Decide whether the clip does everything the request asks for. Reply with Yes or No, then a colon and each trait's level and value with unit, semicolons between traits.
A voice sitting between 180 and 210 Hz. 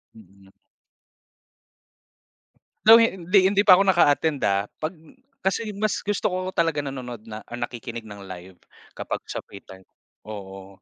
No: low, 130 Hz